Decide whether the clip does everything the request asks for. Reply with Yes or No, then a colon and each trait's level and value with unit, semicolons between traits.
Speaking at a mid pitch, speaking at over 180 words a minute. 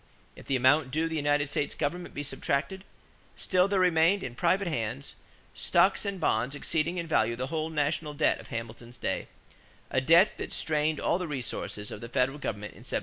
Yes: medium, 145 Hz; average, 195 wpm